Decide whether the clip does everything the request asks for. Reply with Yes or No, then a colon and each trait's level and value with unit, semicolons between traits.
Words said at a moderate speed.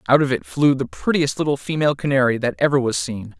No: fast, 230 wpm